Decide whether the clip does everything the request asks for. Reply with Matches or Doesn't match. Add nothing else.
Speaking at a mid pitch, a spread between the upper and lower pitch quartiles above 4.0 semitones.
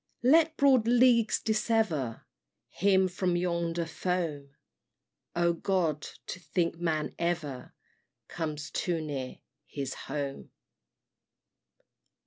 Matches